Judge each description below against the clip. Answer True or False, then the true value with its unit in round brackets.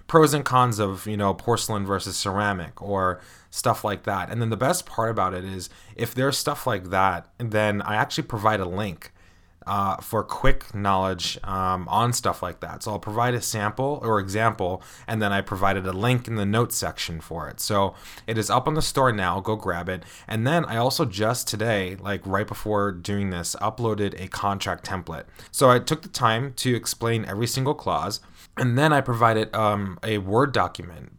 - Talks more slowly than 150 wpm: False (200 wpm)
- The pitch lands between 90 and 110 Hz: True (105 Hz)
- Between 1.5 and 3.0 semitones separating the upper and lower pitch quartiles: False (3.5 semitones)